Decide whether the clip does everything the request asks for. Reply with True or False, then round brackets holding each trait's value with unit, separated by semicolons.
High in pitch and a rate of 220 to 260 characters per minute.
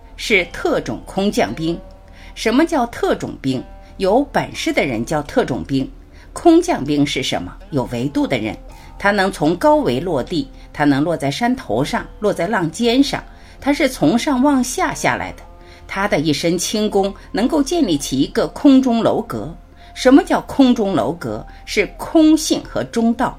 True (220 Hz; 230 characters per minute)